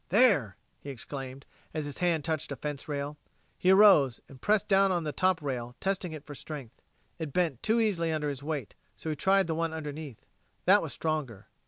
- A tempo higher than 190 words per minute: Yes, average, 200 wpm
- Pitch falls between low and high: Yes, medium, 155 Hz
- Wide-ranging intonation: No, average, 4.2 semitones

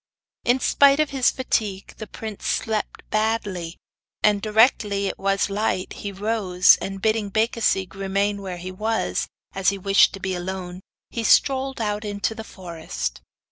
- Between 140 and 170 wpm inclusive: Yes, average, 155 wpm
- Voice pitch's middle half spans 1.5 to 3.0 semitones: Yes, narrow, 2.6 semitones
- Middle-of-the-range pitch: No, high, 205 Hz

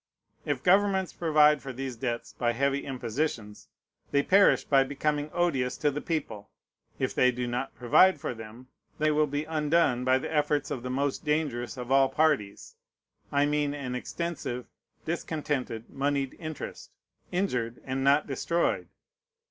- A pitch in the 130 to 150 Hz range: Yes, medium, 140 Hz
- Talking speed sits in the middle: Yes, average, 150 wpm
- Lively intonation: No, average, 3.4 semitones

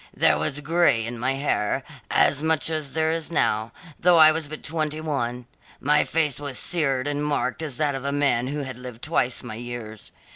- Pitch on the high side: No, medium, 145 Hz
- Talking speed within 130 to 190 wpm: No, fast, 205 wpm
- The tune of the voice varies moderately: Yes, average, 4.0 semitones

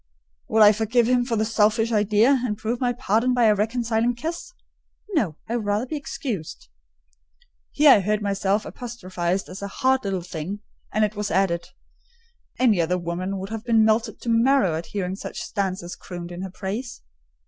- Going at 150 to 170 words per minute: No, average, 180 wpm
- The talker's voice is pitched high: Yes, high, 215 Hz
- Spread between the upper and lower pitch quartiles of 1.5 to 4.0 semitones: Yes, average, 3.7 semitones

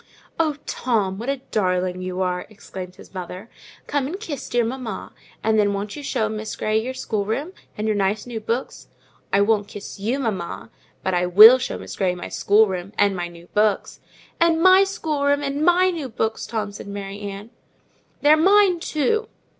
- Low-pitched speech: No, high, 220 Hz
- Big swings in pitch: Yes, wide, 6.2 semitones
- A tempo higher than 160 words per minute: Yes, average, 185 wpm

